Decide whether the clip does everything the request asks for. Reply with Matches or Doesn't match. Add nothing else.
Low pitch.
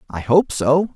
Doesn't match